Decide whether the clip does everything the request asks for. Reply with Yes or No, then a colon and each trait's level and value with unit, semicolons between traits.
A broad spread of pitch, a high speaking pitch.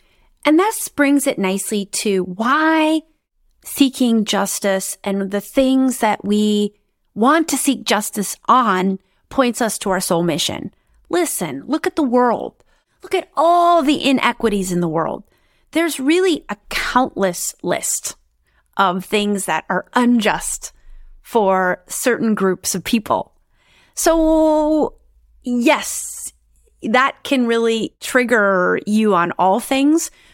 Yes: wide, 6.7 semitones; high, 235 Hz